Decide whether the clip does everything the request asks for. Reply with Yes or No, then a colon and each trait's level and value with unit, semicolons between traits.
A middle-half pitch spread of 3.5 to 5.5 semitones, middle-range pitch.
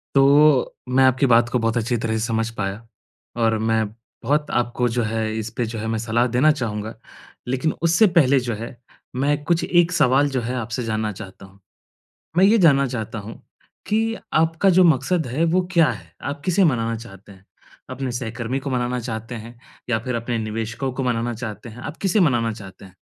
No: average, 4.1 semitones; low, 120 Hz